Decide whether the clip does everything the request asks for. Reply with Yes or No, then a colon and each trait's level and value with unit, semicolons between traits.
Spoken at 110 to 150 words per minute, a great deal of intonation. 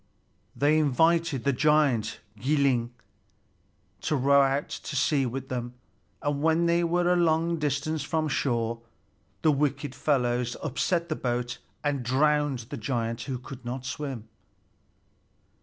No: slow, 135 wpm; average, 3.6 semitones